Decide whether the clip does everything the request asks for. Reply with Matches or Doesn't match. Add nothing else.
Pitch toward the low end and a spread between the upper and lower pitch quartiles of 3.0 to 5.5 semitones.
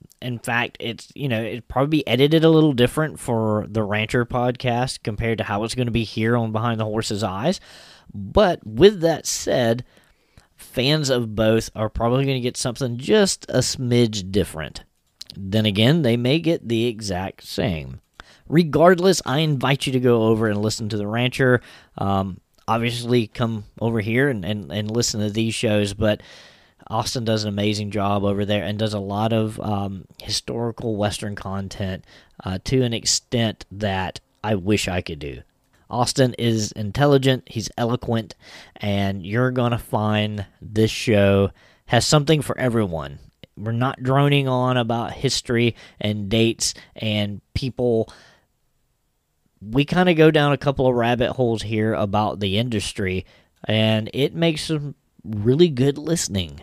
Matches